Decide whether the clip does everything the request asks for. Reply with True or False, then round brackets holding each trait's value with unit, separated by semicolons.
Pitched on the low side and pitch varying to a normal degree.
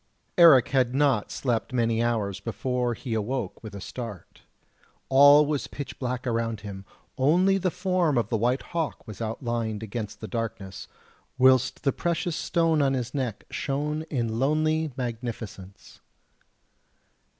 True (125 Hz; 4.2 semitones)